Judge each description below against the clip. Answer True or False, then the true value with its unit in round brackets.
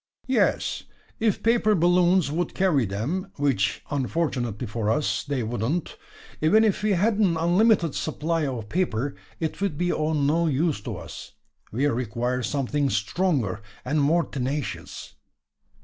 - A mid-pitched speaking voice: True (150 Hz)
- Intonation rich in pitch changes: True (5.8 semitones)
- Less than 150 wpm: True (140 wpm)